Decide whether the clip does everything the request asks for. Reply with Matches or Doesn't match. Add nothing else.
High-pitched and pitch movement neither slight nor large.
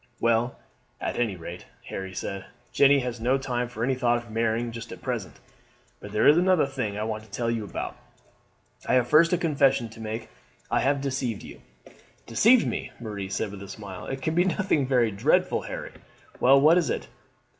Doesn't match